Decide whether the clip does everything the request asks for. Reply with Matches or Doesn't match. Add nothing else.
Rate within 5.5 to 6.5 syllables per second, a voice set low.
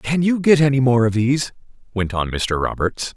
Doesn't match